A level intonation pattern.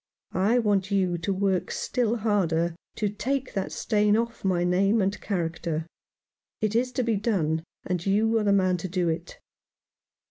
No: average, 3.4 semitones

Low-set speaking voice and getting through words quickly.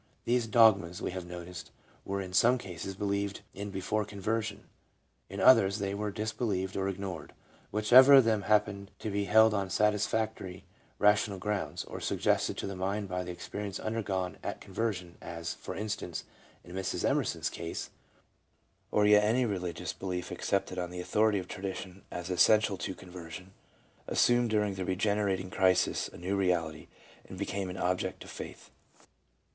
No: low, 100 Hz; average, 160 wpm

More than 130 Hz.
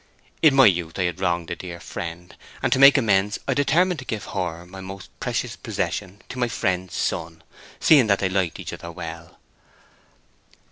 No: very low, 95 Hz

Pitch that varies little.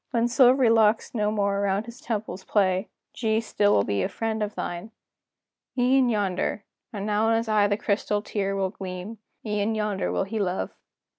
Yes: narrow, 2.2 semitones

